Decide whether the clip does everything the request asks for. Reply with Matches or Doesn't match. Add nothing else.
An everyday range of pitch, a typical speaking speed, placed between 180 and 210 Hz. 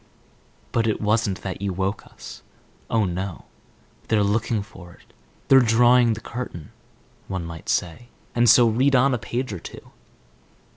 Doesn't match